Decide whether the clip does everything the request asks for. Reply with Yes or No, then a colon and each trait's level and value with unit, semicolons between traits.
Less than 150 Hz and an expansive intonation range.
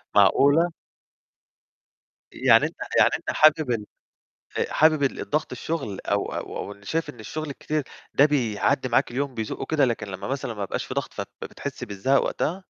Yes: low, 135 Hz; wide, 6.1 semitones